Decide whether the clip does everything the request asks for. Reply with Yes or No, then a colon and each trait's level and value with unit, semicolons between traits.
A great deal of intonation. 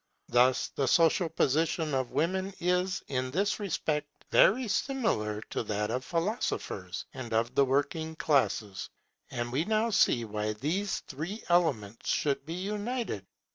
Yes: wide, 7.4 semitones